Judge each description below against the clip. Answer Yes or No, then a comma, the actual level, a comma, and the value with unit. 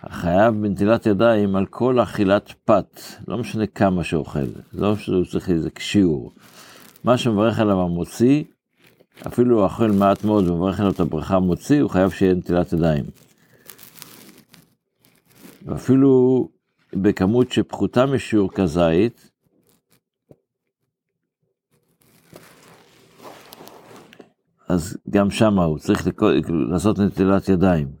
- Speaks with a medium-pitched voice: No, low, 100 Hz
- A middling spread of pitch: Yes, average, 4.0 semitones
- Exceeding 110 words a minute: No, average, 105 wpm